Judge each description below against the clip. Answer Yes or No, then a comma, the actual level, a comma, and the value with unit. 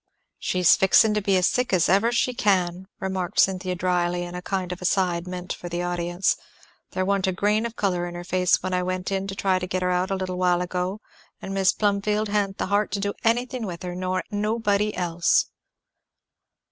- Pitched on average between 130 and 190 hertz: Yes, medium, 185 Hz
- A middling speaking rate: No, fast, 215 wpm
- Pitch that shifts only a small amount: Yes, narrow, 2.0 semitones